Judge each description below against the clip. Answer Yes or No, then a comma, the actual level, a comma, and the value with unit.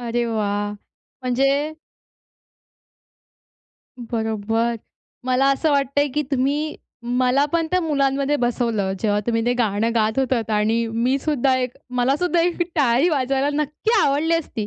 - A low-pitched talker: No, very high, 255 Hz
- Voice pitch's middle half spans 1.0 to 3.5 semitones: No, average, 3.9 semitones